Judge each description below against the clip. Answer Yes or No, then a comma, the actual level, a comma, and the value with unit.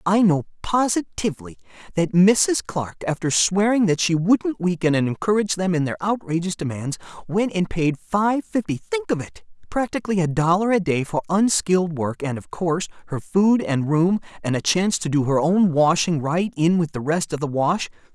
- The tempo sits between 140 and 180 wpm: No, average, 190 wpm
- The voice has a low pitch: No, medium, 175 Hz